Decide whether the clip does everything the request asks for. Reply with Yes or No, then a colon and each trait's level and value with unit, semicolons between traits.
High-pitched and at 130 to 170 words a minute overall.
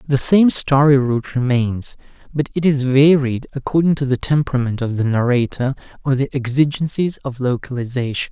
No: low, 135 Hz; average, 150 wpm